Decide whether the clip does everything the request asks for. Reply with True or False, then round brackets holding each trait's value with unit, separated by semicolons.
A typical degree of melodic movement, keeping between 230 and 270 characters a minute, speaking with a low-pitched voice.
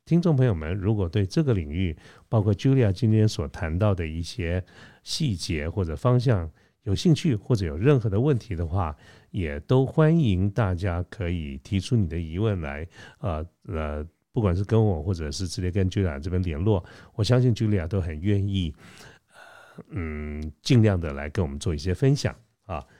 False (4.7 semitones; 285 characters per minute; 95 Hz)